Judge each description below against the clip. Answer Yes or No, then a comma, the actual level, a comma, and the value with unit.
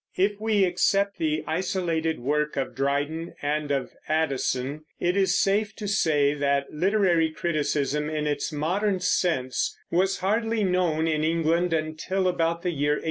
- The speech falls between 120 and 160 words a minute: Yes, average, 150 wpm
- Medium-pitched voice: Yes, medium, 160 Hz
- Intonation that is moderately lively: Yes, average, 3.8 semitones